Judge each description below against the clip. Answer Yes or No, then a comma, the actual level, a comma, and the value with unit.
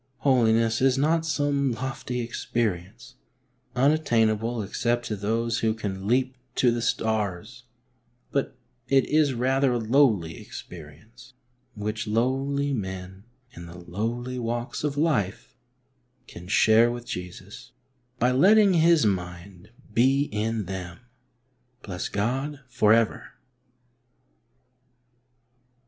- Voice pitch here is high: No, low, 115 Hz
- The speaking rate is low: Yes, slow, 110 wpm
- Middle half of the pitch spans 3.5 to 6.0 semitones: Yes, average, 4.2 semitones